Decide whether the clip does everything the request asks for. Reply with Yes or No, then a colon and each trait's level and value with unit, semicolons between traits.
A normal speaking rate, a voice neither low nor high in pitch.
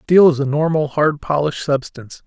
Yes: average, 185 wpm; medium, 145 Hz